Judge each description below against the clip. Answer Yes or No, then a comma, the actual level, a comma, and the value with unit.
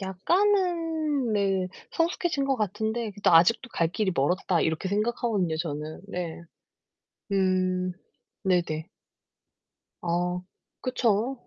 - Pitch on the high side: Yes, high, 195 Hz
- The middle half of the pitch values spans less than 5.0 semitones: No, average, 5.3 semitones